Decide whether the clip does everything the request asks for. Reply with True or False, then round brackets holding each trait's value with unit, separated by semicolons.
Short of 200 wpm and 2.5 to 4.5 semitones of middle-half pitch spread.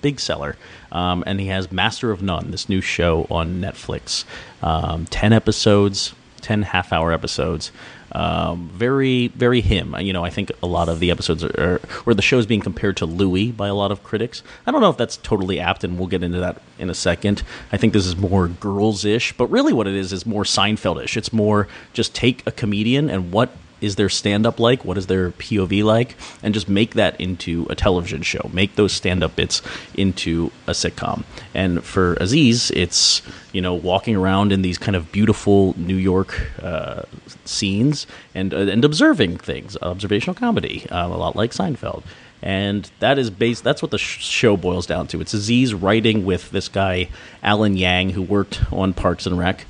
False (205 wpm; 3.2 semitones)